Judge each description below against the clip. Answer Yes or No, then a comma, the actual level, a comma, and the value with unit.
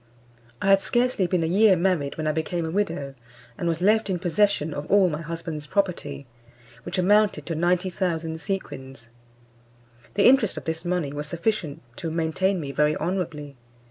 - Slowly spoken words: No, average, 170 wpm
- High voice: No, medium, 170 Hz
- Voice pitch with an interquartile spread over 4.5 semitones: No, average, 3.9 semitones